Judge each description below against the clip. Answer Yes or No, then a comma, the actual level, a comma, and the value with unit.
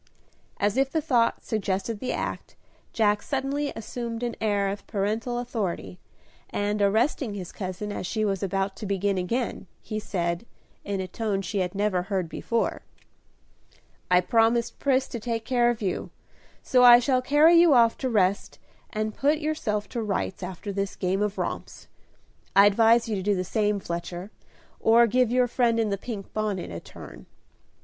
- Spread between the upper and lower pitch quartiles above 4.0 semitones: No, average, 3.5 semitones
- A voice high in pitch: Yes, high, 215 Hz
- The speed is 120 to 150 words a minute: No, average, 170 wpm